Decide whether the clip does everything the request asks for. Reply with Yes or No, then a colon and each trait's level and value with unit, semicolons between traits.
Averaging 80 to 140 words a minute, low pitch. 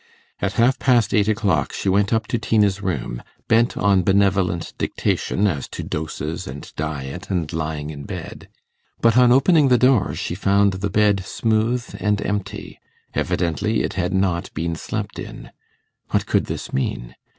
No: average, 160 wpm; low, 100 Hz